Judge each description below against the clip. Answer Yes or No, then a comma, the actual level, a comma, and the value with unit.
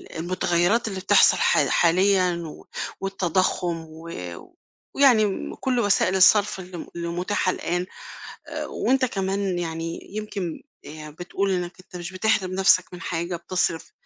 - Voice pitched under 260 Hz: Yes, medium, 185 Hz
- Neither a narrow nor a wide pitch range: No, narrow, 2.3 semitones